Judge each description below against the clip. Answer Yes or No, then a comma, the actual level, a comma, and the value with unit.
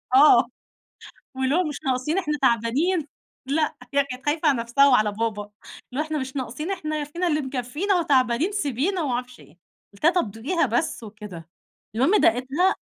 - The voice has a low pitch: No, very high, 275 Hz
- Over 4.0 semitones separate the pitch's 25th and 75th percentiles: Yes, average, 4.6 semitones